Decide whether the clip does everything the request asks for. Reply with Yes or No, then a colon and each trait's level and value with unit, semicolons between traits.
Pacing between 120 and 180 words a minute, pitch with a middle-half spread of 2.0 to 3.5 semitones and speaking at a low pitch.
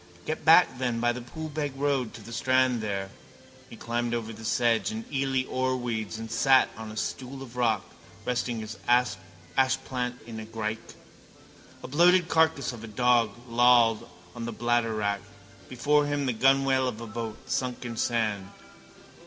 Yes: average, 160 wpm; average, 2.8 semitones; low, 120 Hz